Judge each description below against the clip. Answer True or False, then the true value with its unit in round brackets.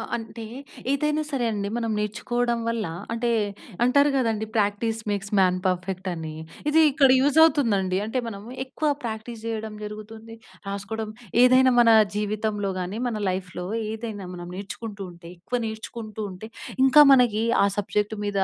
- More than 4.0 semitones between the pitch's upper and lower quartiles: False (3.0 semitones)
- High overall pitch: True (220 Hz)